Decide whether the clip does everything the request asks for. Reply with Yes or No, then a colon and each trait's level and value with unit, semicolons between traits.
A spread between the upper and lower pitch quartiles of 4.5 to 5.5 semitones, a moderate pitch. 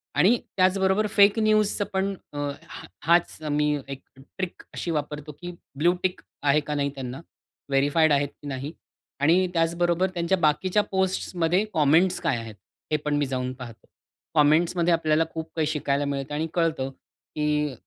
No: average, 3.7 semitones; medium, 160 Hz